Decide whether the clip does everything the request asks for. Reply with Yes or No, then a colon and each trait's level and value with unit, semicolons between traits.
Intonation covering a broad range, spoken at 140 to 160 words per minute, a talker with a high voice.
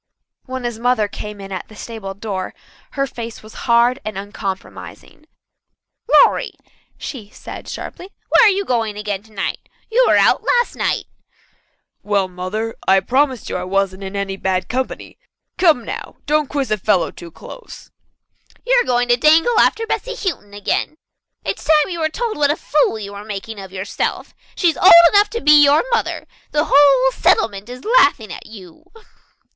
No: wide, 6.8 semitones; average, 175 wpm; high, 230 Hz